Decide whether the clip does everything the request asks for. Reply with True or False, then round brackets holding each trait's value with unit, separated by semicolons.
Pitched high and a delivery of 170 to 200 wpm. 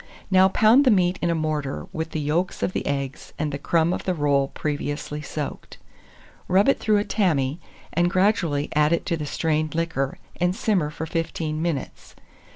False (160 Hz; 185 wpm)